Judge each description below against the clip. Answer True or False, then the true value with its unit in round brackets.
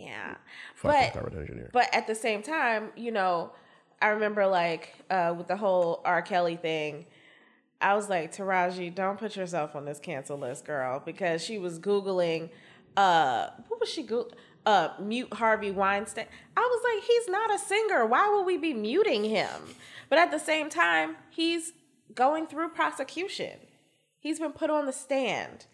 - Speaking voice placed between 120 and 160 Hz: False (215 Hz)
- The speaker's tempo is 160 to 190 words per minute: True (170 wpm)